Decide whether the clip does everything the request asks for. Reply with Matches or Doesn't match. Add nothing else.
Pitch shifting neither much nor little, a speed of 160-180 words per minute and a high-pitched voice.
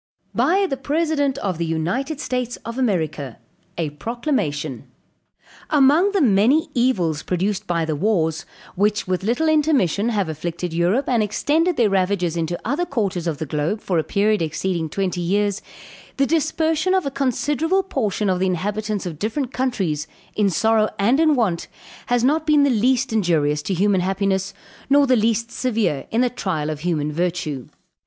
Doesn't match